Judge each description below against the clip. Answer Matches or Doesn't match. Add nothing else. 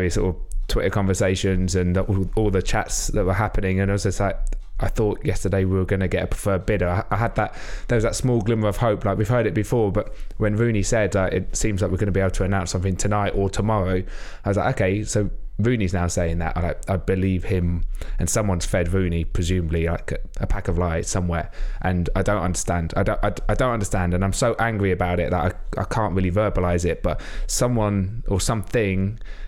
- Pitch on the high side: Doesn't match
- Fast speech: Matches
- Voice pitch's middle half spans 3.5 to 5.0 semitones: Doesn't match